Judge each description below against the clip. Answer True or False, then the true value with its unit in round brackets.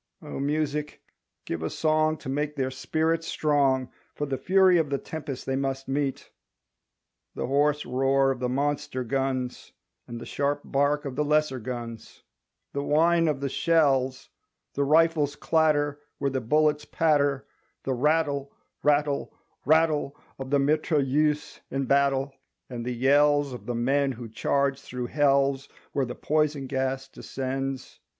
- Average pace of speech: True (150 wpm)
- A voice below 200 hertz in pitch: True (140 Hz)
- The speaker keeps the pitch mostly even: True (2.1 semitones)